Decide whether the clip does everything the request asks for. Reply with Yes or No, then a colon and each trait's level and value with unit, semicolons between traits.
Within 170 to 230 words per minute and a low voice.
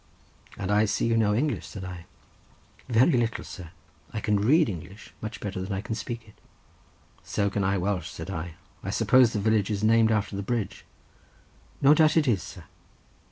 Yes: average, 190 wpm; low, 105 Hz